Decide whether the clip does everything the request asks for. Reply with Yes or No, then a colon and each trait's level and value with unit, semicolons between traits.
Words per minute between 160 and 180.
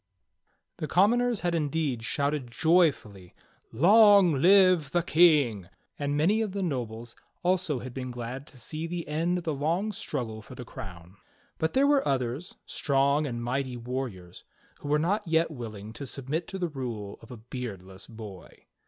Yes: average, 170 wpm